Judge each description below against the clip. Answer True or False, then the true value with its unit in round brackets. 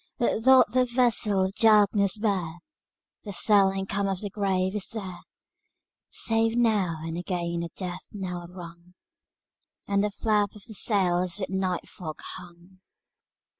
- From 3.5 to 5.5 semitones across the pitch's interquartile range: False (2.9 semitones)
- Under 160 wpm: True (150 wpm)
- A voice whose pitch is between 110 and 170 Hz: False (195 Hz)